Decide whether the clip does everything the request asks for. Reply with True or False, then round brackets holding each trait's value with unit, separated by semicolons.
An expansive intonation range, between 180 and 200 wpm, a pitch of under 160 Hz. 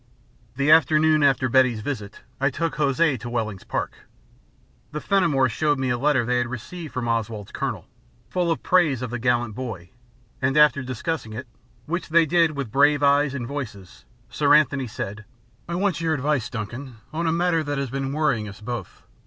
False (4.2 semitones; 185 wpm; 135 Hz)